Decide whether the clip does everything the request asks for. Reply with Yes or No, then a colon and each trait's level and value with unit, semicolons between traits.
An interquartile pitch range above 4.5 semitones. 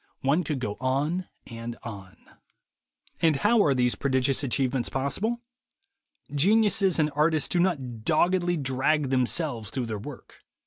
Yes: average, 4.9 semitones